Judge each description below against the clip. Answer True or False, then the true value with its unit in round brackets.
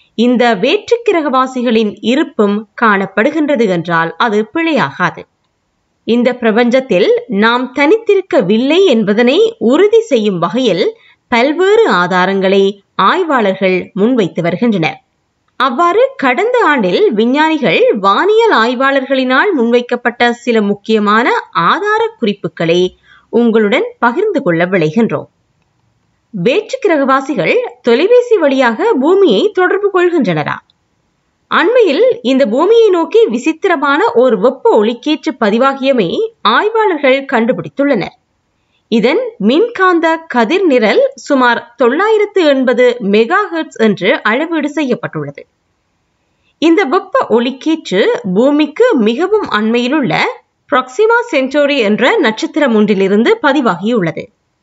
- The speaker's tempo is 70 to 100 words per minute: True (85 wpm)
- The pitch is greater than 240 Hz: True (270 Hz)